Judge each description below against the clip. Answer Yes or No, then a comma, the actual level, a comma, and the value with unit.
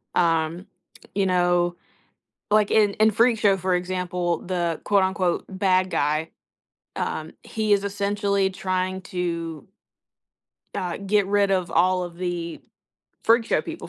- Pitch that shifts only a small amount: Yes, narrow, 2.3 semitones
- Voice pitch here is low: No, medium, 185 Hz